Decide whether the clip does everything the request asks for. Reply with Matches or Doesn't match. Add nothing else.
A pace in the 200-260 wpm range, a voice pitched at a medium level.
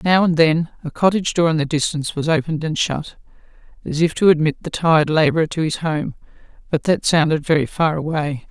Matches